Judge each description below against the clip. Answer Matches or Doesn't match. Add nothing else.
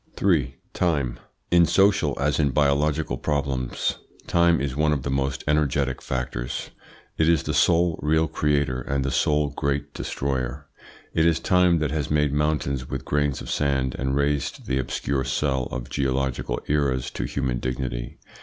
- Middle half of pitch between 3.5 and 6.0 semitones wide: Doesn't match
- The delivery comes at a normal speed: Matches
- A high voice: Doesn't match